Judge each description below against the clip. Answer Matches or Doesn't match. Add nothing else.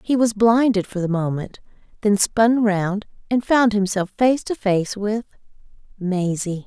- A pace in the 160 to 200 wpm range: Doesn't match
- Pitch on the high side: Matches